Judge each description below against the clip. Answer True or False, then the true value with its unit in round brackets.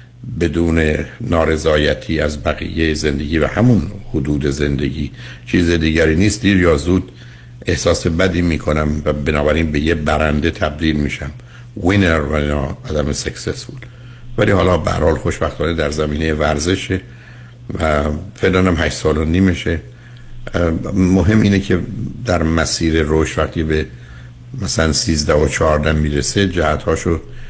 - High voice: False (80 Hz)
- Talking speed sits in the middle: True (125 wpm)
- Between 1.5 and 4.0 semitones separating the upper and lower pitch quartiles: False (4.6 semitones)